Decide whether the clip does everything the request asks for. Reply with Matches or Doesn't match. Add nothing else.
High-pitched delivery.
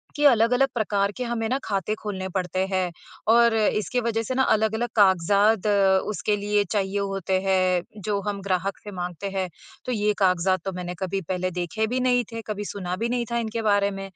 Matches